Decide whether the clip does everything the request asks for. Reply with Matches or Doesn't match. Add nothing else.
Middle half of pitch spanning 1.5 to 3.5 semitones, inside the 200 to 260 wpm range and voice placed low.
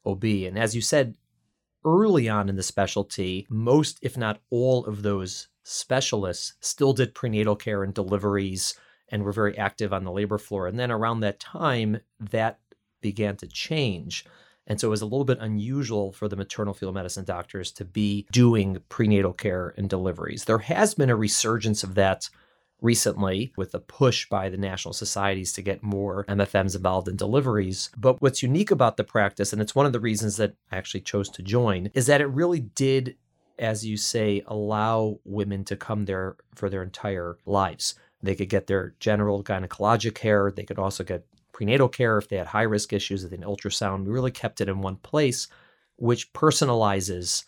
Doesn't match